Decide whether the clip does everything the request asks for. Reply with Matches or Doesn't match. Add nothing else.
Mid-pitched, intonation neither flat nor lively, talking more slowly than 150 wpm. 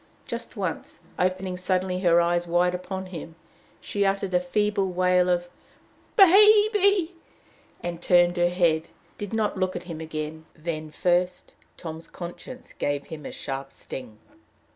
Doesn't match